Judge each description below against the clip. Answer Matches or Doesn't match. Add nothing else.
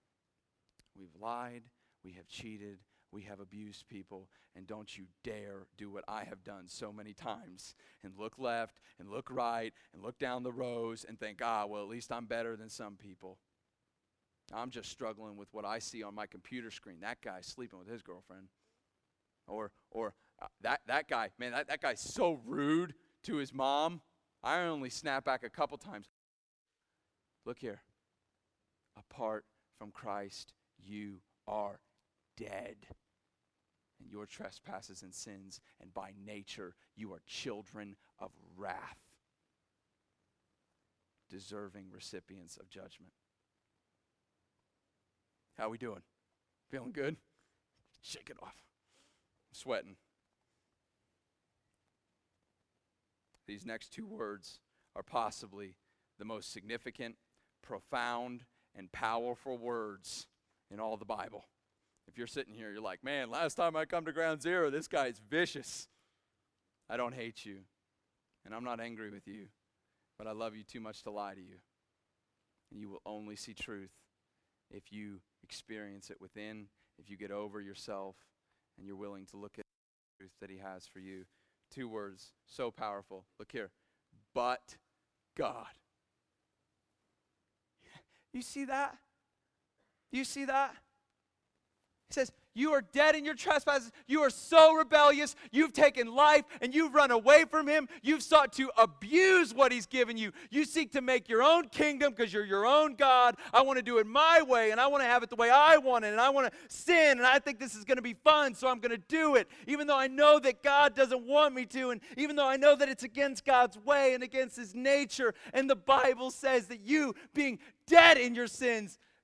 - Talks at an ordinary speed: Matches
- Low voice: Matches